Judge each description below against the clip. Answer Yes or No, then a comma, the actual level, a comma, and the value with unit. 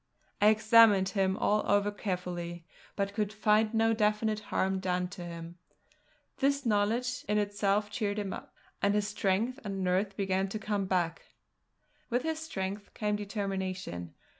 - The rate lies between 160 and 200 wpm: No, average, 150 wpm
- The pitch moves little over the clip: Yes, narrow, 2.1 semitones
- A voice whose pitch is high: Yes, high, 205 Hz